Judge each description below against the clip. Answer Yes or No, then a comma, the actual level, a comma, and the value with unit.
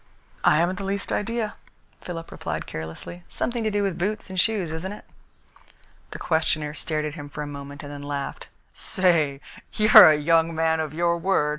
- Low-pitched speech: No, medium, 165 Hz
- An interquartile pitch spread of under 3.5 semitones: No, average, 4.2 semitones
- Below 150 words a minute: No, average, 185 wpm